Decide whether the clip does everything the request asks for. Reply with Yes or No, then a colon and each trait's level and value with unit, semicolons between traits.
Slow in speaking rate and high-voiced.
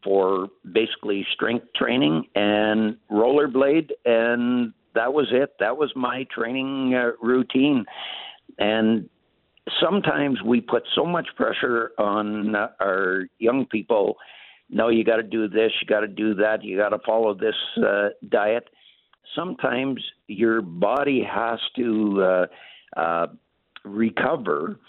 No: slow, 130 wpm; low, 115 Hz